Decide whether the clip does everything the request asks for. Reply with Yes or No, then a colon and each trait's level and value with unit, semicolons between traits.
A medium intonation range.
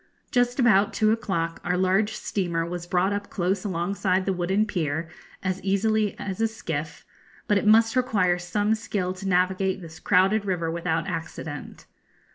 Yes: average, 3.1 semitones